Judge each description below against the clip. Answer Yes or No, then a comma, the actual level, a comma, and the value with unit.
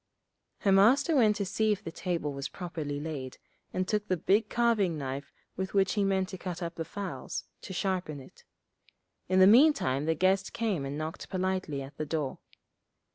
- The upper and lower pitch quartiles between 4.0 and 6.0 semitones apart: Yes, average, 4.6 semitones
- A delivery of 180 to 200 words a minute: Yes, average, 185 wpm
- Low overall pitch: No, medium, 185 Hz